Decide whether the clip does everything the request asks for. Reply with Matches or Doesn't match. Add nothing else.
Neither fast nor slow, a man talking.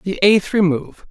Matches